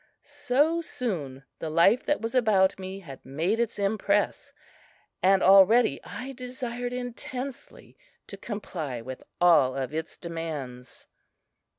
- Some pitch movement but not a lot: No, wide, 7.4 semitones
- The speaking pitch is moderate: No, high, 195 Hz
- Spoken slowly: Yes, slow, 120 wpm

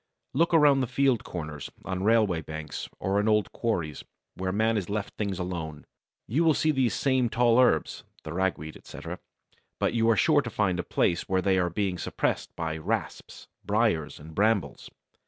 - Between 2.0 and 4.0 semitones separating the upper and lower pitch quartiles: No, wide, 5.4 semitones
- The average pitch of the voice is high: No, low, 100 Hz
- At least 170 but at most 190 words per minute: Yes, average, 180 wpm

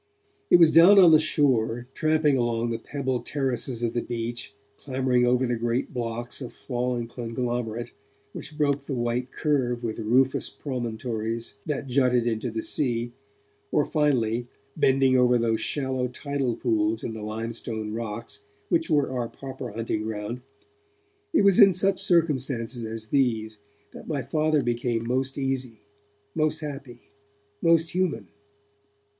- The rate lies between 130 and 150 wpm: Yes, average, 145 wpm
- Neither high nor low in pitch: No, low, 125 Hz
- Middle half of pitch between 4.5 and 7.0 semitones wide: No, average, 3.3 semitones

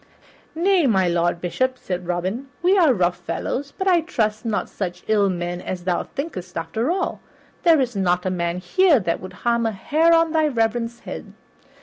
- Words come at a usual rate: Yes, average, 190 wpm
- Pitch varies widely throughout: Yes, wide, 8.8 semitones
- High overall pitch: Yes, high, 220 Hz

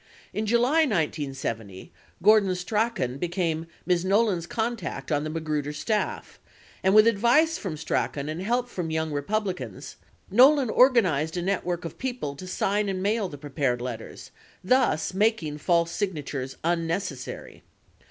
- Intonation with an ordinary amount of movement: No, wide, 6.1 semitones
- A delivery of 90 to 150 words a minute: Yes, average, 145 wpm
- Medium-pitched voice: Yes, medium, 180 Hz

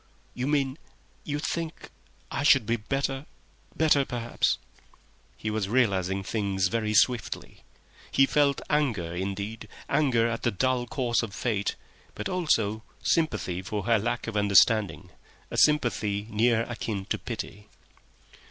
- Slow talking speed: Yes, slow, 125 wpm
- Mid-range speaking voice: No, low, 115 Hz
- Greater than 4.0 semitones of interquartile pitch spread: Yes, average, 4.7 semitones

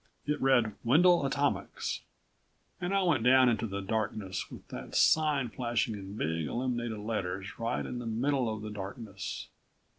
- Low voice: Yes, low, 115 Hz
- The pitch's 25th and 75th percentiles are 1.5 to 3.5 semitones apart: No, average, 4.2 semitones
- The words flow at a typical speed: Yes, average, 155 wpm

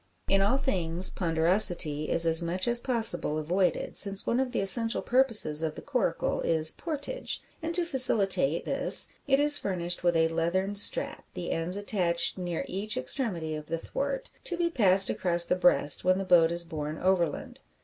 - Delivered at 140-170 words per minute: No, average, 180 wpm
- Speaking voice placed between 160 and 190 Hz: Yes, medium, 185 Hz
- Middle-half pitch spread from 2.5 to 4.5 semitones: No, wide, 5.5 semitones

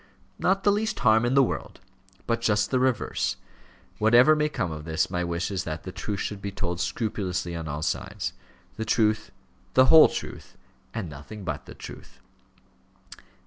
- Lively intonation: Yes, wide, 6.1 semitones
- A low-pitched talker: Yes, low, 105 Hz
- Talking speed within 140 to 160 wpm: No, average, 175 wpm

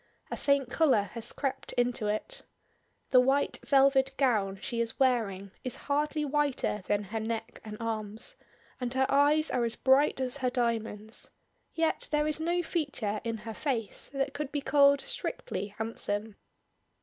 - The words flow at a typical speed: Yes, average, 160 wpm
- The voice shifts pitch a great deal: No, average, 4.3 semitones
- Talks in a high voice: Yes, very high, 255 Hz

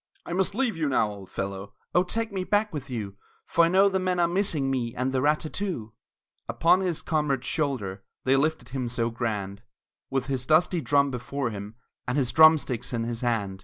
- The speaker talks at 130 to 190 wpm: No, fast, 205 wpm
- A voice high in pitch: No, low, 135 Hz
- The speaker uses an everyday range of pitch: No, wide, 6.5 semitones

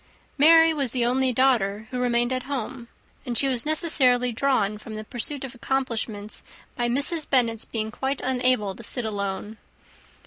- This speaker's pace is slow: No, average, 165 wpm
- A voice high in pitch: Yes, high, 245 Hz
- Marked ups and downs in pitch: No, average, 3.3 semitones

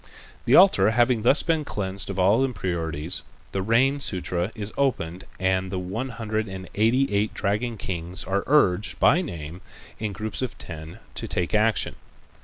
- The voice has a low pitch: Yes, low, 100 Hz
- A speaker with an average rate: Yes, average, 165 wpm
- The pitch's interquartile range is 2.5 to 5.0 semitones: Yes, average, 4.5 semitones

